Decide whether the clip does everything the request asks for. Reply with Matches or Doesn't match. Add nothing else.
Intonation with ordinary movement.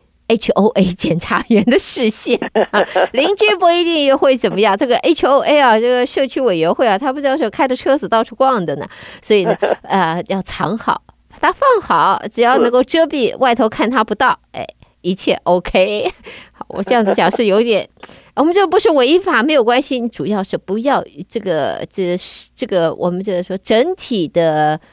Doesn't match